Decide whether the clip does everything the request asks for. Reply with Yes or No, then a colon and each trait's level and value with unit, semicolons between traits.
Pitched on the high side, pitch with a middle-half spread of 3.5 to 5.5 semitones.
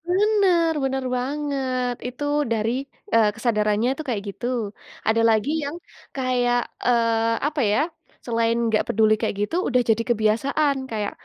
Yes: high, 245 Hz; average, 3.8 semitones